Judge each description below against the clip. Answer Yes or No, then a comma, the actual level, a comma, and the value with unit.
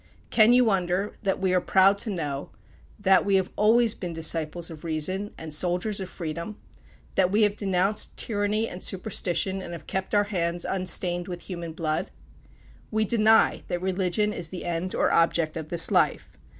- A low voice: No, medium, 185 Hz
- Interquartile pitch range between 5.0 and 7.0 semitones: No, average, 3.2 semitones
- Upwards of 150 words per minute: Yes, average, 175 wpm